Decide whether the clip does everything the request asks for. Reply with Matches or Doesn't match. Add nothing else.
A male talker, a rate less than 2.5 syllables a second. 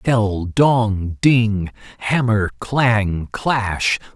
Matches